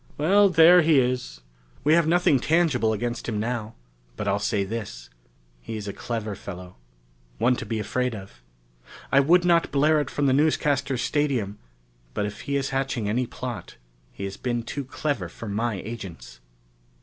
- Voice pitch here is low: Yes, low, 120 Hz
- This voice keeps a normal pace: Yes, average, 170 wpm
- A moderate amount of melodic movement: No, wide, 5.8 semitones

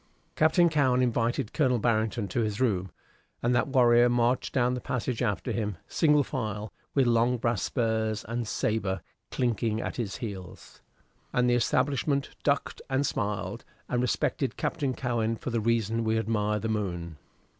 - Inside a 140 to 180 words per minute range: Yes, average, 155 wpm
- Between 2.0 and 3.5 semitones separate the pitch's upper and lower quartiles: Yes, average, 2.8 semitones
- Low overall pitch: Yes, low, 115 Hz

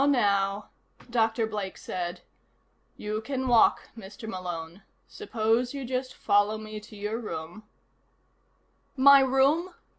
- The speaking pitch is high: Yes, high, 220 Hz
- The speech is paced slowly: Yes, slow, 125 wpm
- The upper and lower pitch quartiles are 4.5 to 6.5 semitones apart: No, average, 4.1 semitones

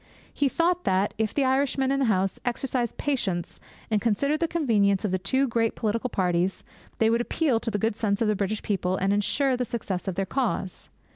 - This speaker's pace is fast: Yes, fast, 210 wpm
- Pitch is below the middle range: No, high, 225 Hz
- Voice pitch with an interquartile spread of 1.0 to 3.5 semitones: No, average, 5.2 semitones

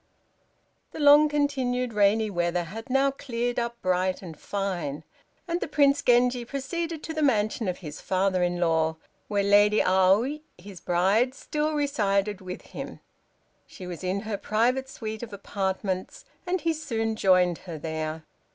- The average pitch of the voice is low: No, high, 210 Hz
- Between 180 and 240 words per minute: No, average, 155 wpm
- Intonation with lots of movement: Yes, wide, 6.3 semitones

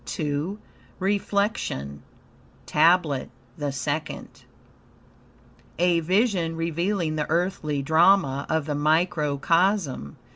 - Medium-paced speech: No, slow, 80 wpm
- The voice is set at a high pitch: No, medium, 160 Hz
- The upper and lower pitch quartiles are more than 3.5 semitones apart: Yes, average, 3.9 semitones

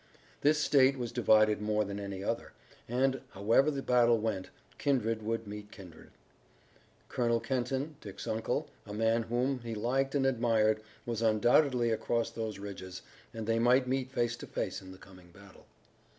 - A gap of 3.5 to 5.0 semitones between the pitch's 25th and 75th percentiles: No, average, 3.1 semitones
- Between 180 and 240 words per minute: No, average, 165 wpm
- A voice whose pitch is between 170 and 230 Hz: No, low, 115 Hz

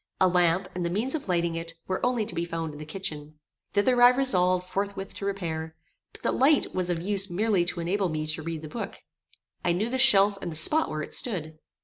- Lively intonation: No, average, 3.7 semitones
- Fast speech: Yes, fast, 235 wpm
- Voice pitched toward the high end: No, medium, 180 Hz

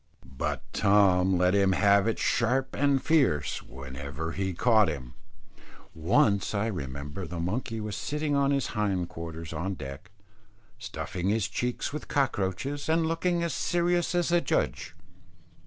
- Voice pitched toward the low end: Yes, low, 100 Hz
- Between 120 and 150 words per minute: Yes, average, 145 wpm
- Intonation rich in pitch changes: Yes, wide, 8.1 semitones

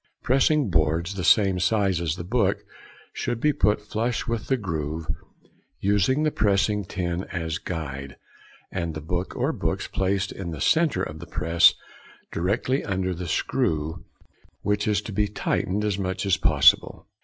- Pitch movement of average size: Yes, average, 3.7 semitones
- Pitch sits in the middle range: No, very low, 95 Hz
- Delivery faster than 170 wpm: No, average, 160 wpm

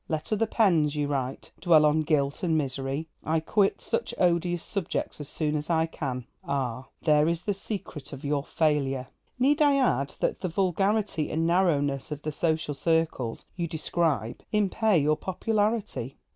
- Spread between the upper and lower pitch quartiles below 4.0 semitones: No, average, 4.3 semitones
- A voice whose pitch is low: No, medium, 160 Hz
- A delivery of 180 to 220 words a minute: No, average, 165 wpm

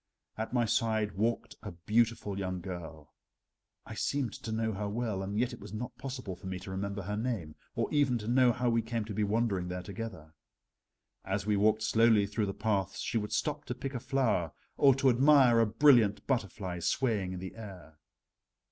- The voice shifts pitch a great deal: No, average, 3.6 semitones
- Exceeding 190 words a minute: Yes, average, 200 wpm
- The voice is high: No, low, 110 Hz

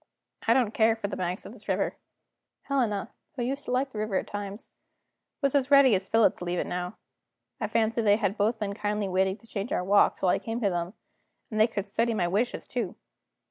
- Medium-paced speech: No, fast, 230 wpm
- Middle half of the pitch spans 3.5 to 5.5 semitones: No, average, 2.9 semitones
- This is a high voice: Yes, high, 215 Hz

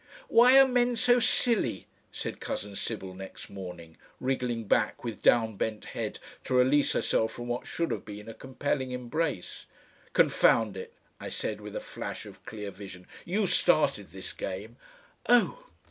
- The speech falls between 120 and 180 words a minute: Yes, average, 160 wpm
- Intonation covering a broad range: Yes, wide, 8.4 semitones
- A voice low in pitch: Yes, low, 120 Hz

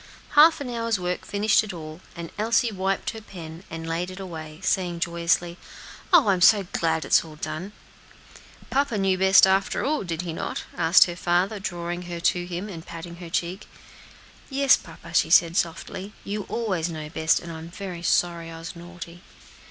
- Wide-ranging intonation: No, average, 2.9 semitones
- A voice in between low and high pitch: Yes, medium, 175 Hz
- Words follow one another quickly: No, average, 190 wpm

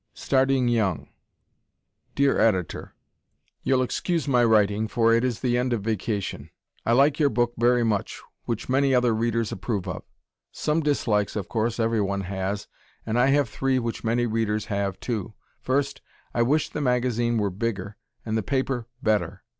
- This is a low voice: Yes, low, 115 Hz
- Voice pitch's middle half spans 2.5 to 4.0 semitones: Yes, average, 3.2 semitones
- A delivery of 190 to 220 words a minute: No, average, 160 wpm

